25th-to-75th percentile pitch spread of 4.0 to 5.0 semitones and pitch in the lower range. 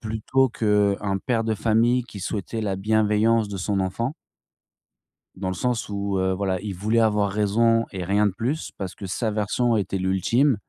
No: average, 2.8 semitones; low, 105 Hz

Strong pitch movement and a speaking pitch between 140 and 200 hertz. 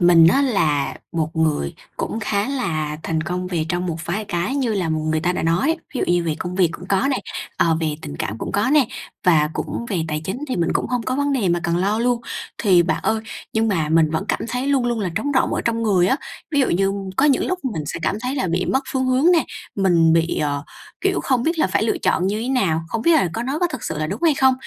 Yes: wide, 7.4 semitones; high, 190 Hz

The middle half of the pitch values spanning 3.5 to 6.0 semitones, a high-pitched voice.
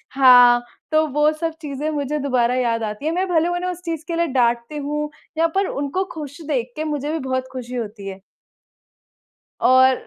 Yes: average, 3.9 semitones; very high, 285 Hz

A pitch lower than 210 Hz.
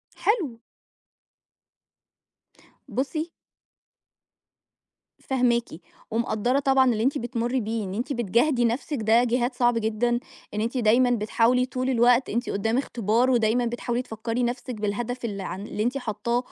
No: high, 240 Hz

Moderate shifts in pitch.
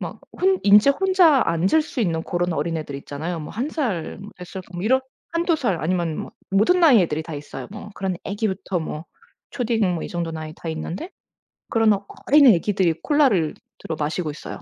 No: wide, 6.8 semitones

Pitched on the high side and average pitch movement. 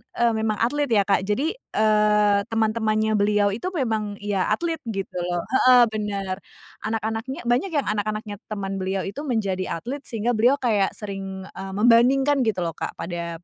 Yes: high, 215 Hz; average, 3.3 semitones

